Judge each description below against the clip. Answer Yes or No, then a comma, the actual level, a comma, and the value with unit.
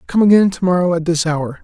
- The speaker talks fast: Yes, fast, 260 wpm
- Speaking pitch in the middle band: Yes, medium, 170 Hz